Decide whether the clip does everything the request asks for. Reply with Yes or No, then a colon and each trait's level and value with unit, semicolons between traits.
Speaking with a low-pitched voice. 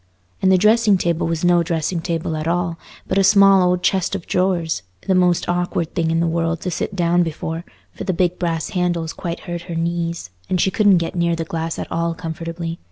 No: medium, 170 Hz